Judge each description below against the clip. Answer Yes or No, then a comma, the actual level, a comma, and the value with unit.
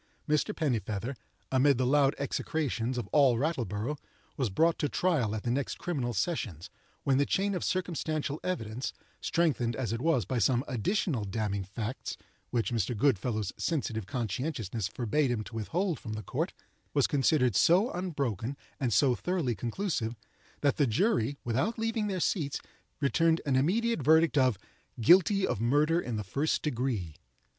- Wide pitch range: Yes, wide, 6.0 semitones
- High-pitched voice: No, low, 130 Hz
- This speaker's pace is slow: No, average, 155 wpm